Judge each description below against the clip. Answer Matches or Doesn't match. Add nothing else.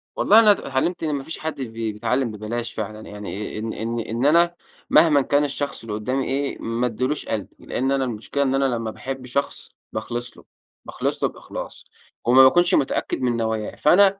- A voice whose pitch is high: Doesn't match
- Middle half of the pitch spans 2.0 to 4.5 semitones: Matches